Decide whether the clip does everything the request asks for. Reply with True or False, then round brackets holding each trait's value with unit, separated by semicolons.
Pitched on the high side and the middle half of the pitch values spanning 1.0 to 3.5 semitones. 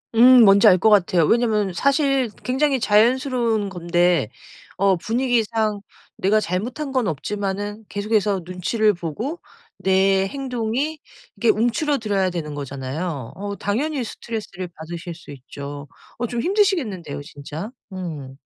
False (205 Hz; 5.4 semitones)